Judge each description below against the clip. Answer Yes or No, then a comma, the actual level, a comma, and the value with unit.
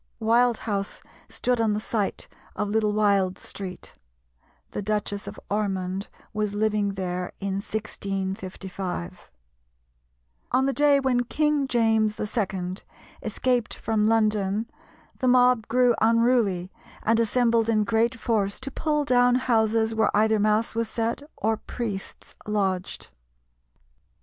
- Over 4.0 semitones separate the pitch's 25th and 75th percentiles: No, average, 2.7 semitones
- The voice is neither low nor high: No, high, 220 Hz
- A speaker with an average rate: No, slow, 125 wpm